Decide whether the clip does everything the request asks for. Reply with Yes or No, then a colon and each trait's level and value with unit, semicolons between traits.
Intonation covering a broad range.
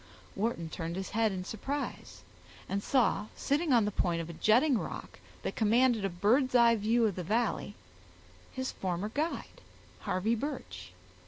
No: average, 4.5 semitones